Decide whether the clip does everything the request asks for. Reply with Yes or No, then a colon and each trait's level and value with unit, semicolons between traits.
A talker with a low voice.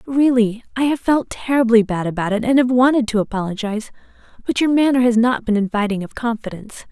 No: high, 235 Hz